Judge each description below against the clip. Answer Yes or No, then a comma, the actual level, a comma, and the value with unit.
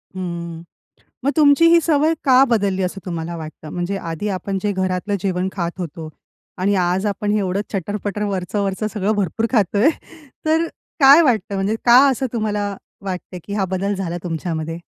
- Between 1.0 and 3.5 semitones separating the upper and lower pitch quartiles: Yes, average, 2.9 semitones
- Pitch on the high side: Yes, high, 195 Hz